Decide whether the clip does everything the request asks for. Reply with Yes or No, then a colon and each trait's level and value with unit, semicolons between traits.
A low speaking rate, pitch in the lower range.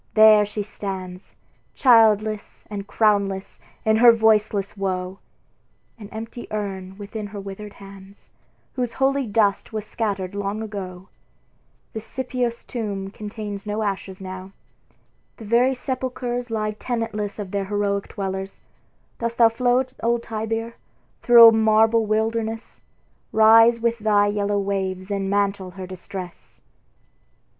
No: slow, 125 wpm; high, 210 Hz